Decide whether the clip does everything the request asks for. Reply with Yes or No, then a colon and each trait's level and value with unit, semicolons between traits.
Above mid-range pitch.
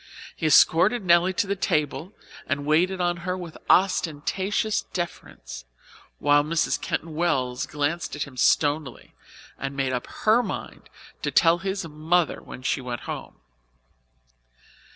No: medium, 160 Hz